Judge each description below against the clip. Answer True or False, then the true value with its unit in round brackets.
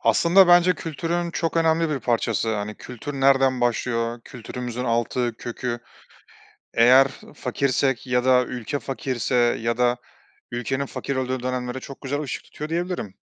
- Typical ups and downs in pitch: True (3.0 semitones)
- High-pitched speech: False (130 Hz)